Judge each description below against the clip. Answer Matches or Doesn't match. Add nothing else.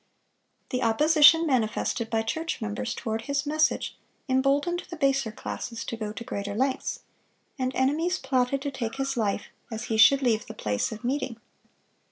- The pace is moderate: Matches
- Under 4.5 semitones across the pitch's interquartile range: Matches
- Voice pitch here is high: Matches